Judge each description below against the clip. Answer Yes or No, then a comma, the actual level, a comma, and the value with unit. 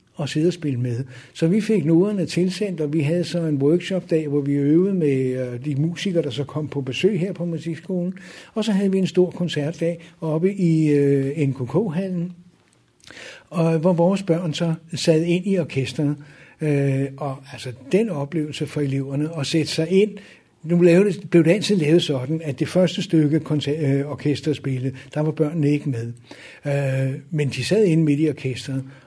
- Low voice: No, medium, 155 Hz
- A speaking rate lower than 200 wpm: Yes, average, 175 wpm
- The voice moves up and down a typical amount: Yes, average, 3.7 semitones